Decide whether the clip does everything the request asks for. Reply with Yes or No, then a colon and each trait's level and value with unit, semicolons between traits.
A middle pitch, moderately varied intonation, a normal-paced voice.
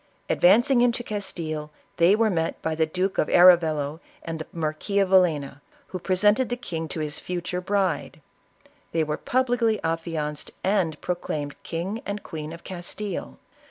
Yes: medium, 175 Hz; average, 4.3 semitones; average, 155 wpm